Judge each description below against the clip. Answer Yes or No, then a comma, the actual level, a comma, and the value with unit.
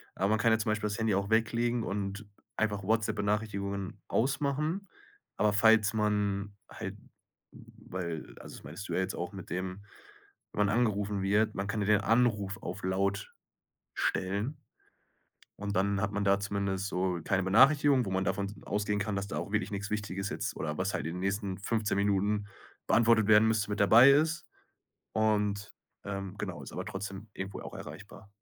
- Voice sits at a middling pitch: No, low, 100 Hz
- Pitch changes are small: Yes, narrow, 1.9 semitones